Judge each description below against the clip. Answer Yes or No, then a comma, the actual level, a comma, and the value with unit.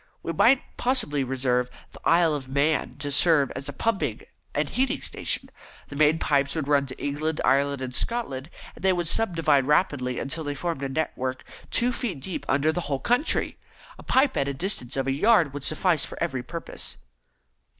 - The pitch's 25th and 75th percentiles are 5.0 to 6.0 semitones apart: No, average, 4.1 semitones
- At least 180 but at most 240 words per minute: Yes, average, 185 wpm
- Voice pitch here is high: No, medium, 145 Hz